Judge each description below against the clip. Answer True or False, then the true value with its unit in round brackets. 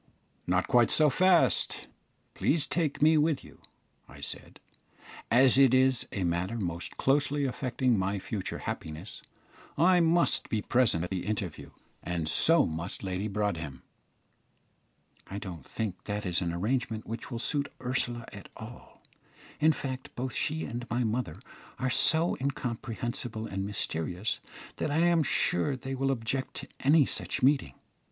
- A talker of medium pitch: False (120 Hz)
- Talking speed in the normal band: True (150 wpm)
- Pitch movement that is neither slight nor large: False (6.1 semitones)